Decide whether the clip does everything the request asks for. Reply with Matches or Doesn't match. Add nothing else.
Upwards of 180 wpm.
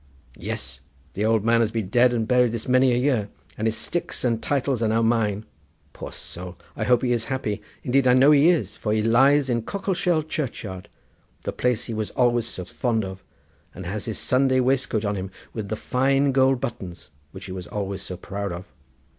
Matches